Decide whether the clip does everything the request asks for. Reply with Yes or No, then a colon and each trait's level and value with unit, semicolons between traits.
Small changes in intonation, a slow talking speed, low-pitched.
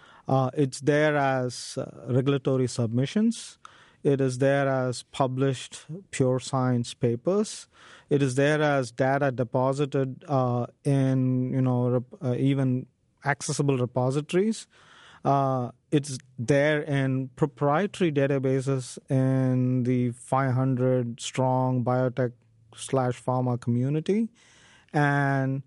Yes: narrow, 1.9 semitones; slow, 105 wpm; low, 130 Hz